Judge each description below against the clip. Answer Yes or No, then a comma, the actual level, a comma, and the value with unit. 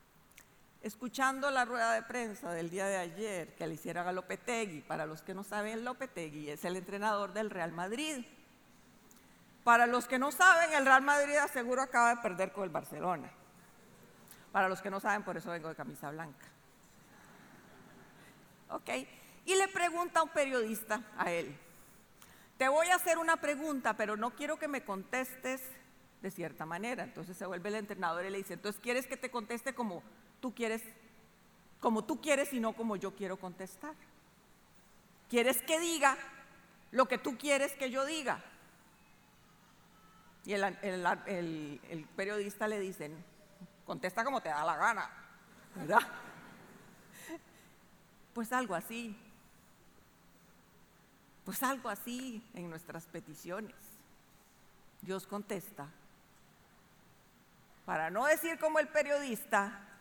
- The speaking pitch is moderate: No, high, 215 Hz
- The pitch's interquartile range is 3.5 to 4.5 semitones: No, wide, 5.6 semitones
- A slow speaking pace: No, average, 145 wpm